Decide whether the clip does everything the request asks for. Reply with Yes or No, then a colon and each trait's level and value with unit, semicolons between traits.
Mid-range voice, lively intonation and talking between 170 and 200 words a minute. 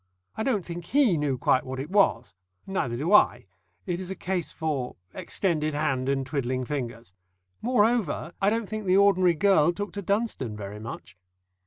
Yes: medium, 170 Hz; wide, 7.3 semitones; average, 175 wpm